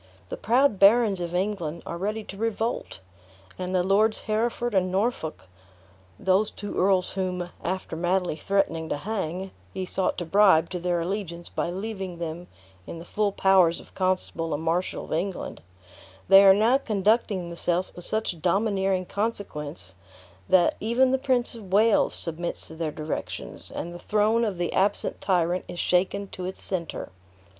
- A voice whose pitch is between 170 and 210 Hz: Yes, high, 190 Hz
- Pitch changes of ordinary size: Yes, average, 3.3 semitones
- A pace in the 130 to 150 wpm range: No, average, 165 wpm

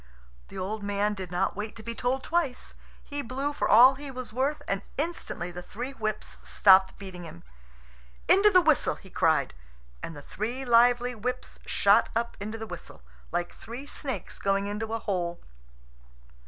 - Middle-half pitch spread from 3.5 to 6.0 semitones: Yes, average, 4.9 semitones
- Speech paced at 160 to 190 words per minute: Yes, average, 170 wpm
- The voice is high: Yes, high, 225 Hz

